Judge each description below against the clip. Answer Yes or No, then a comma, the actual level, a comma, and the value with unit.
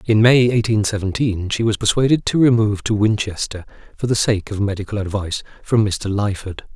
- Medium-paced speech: Yes, average, 180 wpm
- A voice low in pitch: Yes, low, 105 Hz